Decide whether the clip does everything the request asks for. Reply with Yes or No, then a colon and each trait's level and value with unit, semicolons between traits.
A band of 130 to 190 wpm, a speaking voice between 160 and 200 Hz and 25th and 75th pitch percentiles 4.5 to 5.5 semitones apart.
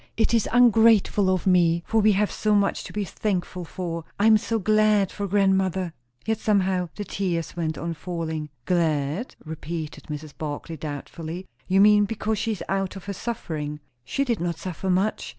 No: average, 180 wpm; high, 190 Hz; average, 3.9 semitones